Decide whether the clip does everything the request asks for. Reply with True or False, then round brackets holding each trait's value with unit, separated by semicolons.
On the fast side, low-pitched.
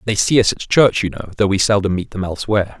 True (280 wpm; 100 Hz)